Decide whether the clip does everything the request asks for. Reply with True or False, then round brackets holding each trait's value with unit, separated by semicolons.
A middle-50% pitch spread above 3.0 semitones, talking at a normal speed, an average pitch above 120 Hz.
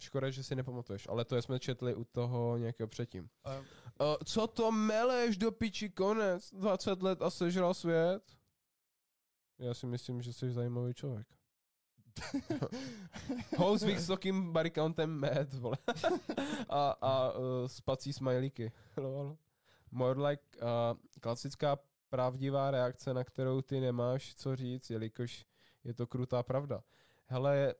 True (5.6 semitones; 125 wpm; 135 Hz)